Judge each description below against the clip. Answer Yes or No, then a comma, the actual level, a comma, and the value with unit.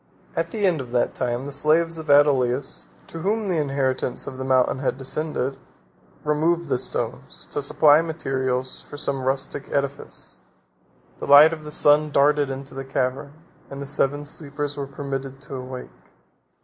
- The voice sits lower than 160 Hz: Yes, medium, 140 Hz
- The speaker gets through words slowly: No, average, 165 wpm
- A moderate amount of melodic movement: No, narrow, 2.3 semitones